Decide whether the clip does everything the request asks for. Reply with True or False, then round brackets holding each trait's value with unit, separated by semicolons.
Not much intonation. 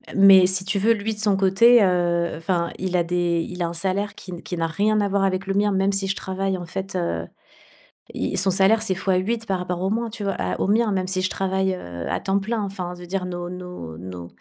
True (2.0 semitones)